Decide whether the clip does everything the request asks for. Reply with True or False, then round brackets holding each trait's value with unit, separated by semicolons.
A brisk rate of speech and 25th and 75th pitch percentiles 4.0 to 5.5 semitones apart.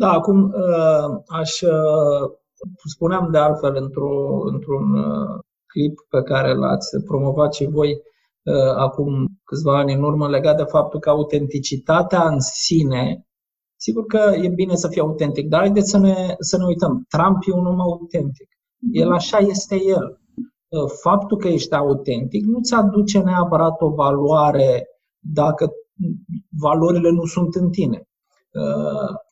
False (135 wpm; 4.6 semitones)